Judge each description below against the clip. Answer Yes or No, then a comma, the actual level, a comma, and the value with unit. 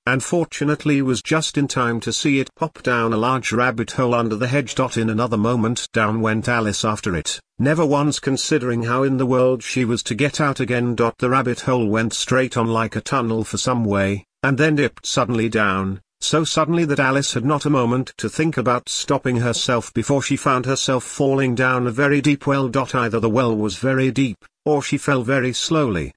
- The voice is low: Yes, low, 125 Hz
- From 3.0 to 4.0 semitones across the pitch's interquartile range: Yes, average, 3.4 semitones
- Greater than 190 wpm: Yes, average, 200 wpm